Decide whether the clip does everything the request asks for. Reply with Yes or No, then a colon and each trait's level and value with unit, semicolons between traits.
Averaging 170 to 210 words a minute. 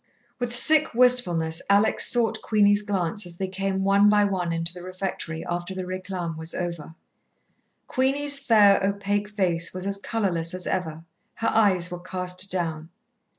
No: average, 155 wpm